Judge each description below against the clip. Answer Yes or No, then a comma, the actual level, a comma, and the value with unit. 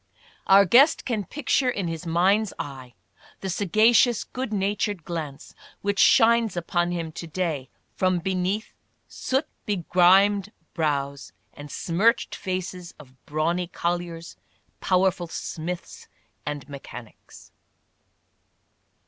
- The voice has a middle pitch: Yes, medium, 180 Hz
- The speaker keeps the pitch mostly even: No, average, 3.8 semitones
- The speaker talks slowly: Yes, slow, 105 wpm